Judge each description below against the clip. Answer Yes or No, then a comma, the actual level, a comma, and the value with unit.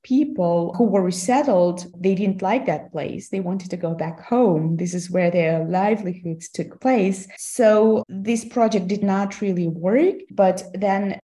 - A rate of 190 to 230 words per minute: No, average, 165 wpm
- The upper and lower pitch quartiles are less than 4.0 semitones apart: Yes, average, 3.3 semitones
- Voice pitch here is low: No, high, 195 Hz